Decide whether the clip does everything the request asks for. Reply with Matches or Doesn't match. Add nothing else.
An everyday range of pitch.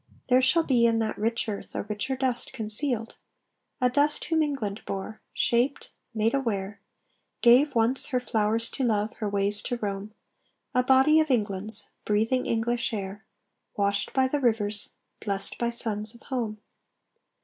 Matches